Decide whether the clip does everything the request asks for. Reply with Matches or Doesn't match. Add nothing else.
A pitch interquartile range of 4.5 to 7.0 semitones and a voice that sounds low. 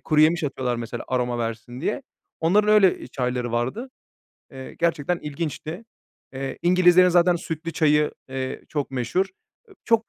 Doesn't match